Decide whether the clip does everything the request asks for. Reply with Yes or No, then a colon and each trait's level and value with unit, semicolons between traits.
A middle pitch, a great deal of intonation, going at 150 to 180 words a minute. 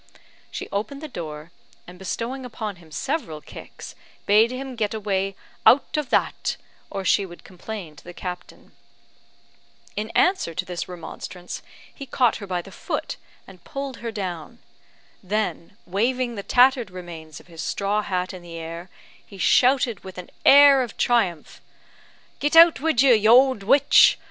No: high, 205 Hz; wide, 6.0 semitones; average, 160 wpm